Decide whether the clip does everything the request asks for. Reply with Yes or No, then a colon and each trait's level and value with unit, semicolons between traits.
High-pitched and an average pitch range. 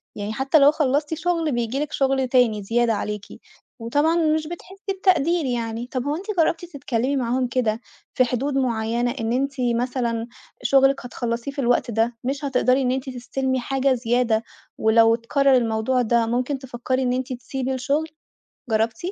Yes: very high, 255 Hz; average, 3.0 semitones